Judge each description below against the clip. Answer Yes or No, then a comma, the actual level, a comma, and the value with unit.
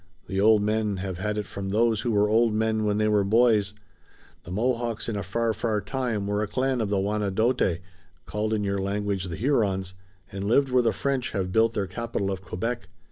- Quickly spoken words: Yes, fast, 210 wpm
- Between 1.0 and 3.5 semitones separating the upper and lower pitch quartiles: Yes, narrow, 2.6 semitones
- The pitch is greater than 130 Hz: No, low, 105 Hz